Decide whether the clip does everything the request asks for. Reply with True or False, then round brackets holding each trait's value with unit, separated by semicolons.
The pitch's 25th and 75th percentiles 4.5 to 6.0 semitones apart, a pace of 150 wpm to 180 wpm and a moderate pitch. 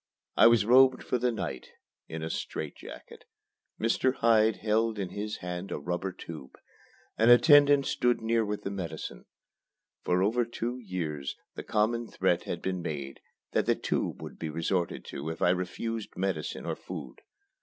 False (4.9 semitones; 165 wpm; 105 Hz)